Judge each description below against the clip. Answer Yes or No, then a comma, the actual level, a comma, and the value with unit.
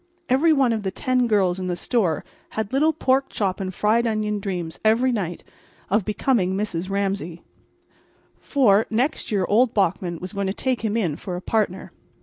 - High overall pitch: Yes, high, 210 Hz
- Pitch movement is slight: No, average, 4.0 semitones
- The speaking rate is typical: Yes, average, 180 wpm